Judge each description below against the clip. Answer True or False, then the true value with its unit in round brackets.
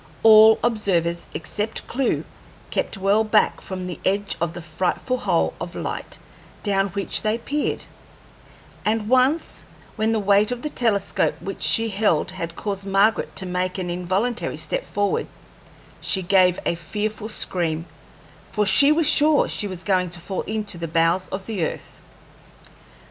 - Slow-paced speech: False (155 wpm)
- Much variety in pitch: False (3.3 semitones)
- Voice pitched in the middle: False (200 Hz)